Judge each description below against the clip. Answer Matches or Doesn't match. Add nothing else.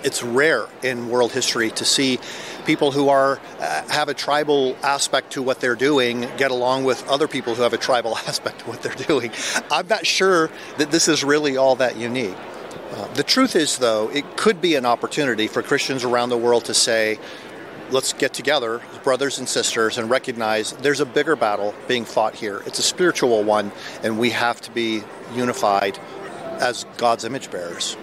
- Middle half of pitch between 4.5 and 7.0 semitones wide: Doesn't match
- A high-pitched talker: Doesn't match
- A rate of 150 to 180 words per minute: Doesn't match